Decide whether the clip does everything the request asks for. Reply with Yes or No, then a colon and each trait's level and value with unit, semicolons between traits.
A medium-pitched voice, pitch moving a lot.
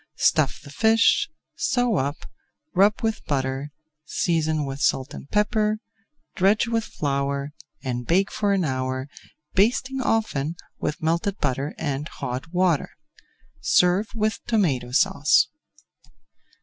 Yes: medium, 165 Hz; wide, 7.3 semitones